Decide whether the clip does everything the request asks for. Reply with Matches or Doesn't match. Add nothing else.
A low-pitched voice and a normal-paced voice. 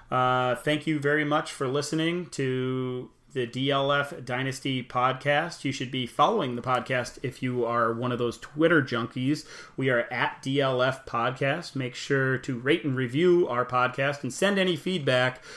Matches